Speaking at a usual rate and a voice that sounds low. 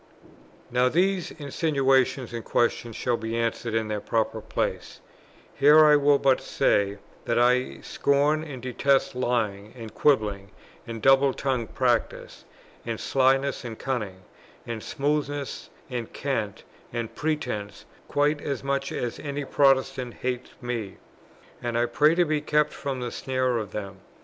Yes: average, 145 wpm; low, 130 Hz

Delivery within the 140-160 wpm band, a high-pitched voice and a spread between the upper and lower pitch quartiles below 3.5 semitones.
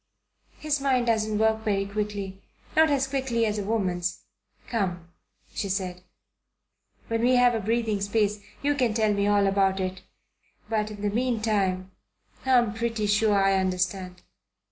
Yes: average, 150 wpm; high, 210 Hz; average, 2.9 semitones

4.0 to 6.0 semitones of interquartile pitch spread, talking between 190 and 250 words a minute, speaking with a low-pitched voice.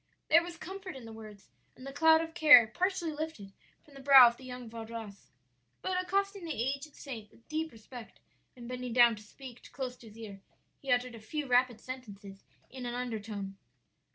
No: average, 5.3 semitones; average, 195 wpm; very high, 250 Hz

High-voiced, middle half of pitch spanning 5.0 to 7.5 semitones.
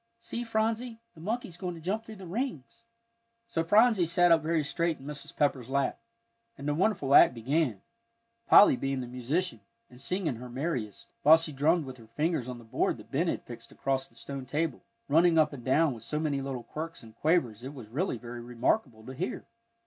No: medium, 150 Hz; wide, 5.4 semitones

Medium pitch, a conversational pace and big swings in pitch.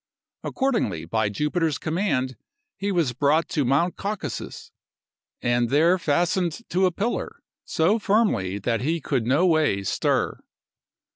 No: medium, 155 Hz; slow, 130 wpm; wide, 7.0 semitones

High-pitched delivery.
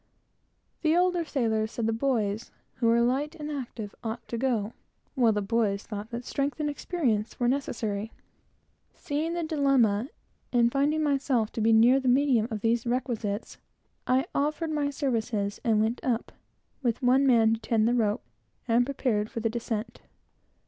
Yes: high, 240 Hz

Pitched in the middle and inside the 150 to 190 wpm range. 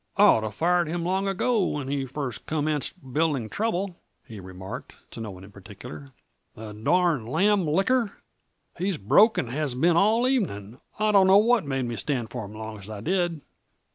Yes: medium, 150 Hz; average, 185 wpm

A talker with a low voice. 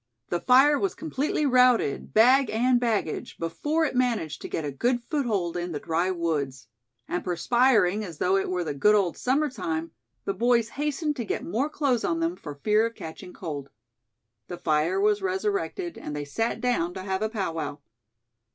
No: high, 215 Hz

